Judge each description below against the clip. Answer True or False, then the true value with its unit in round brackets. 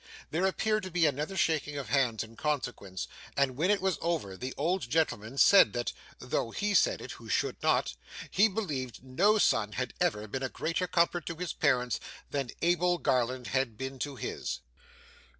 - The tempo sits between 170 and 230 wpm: True (185 wpm)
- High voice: False (140 Hz)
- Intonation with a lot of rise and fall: True (6.1 semitones)